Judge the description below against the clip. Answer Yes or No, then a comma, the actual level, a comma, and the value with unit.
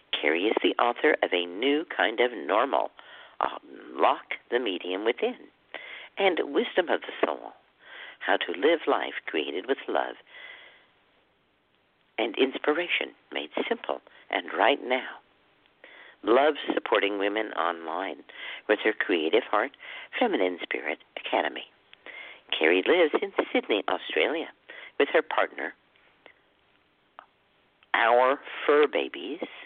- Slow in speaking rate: Yes, slow, 115 wpm